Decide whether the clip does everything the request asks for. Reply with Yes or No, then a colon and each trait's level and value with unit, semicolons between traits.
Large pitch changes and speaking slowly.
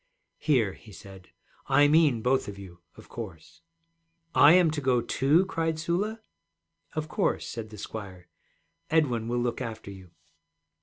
No: wide, 7.2 semitones; average, 150 wpm